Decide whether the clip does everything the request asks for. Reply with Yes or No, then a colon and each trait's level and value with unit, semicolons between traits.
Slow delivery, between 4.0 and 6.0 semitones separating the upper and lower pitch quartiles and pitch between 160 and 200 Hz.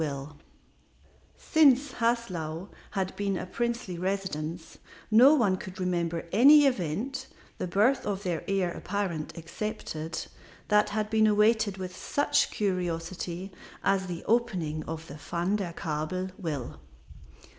Yes: slow, 125 wpm; average, 4.4 semitones; high, 190 Hz